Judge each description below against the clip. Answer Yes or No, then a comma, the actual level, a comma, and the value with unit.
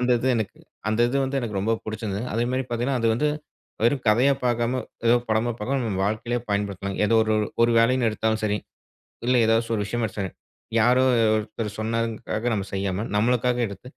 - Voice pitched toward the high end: No, low, 115 Hz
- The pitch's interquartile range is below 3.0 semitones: Yes, narrow, 2.4 semitones